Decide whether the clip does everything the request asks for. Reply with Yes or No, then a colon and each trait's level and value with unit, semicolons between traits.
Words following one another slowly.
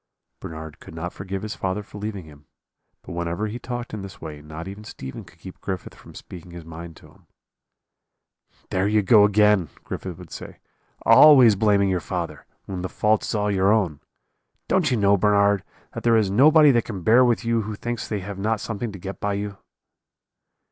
No: average, 200 wpm